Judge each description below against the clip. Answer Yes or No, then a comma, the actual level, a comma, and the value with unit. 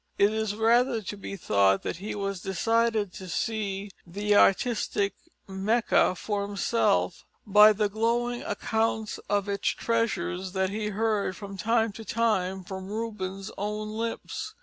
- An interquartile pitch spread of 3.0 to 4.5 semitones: No, narrow, 2.6 semitones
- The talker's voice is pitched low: No, high, 210 Hz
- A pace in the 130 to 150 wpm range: Yes, average, 145 wpm